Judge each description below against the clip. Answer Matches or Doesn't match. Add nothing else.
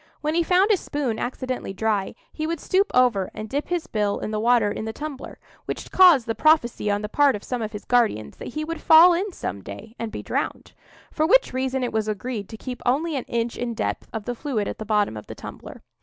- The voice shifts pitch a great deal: Matches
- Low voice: Doesn't match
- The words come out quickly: Matches